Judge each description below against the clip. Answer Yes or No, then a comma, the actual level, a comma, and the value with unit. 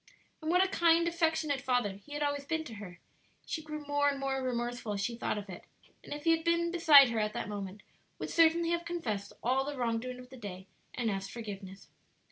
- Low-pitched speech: No, very high, 265 Hz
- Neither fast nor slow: No, fast, 230 wpm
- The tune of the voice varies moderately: No, wide, 7.0 semitones